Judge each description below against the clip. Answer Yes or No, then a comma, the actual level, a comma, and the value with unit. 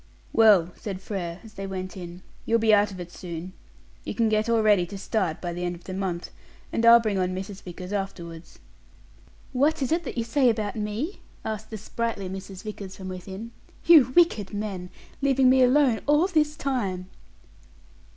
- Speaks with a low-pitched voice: No, high, 205 Hz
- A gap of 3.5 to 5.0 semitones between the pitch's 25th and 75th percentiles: Yes, average, 4.0 semitones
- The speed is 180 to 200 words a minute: Yes, average, 185 wpm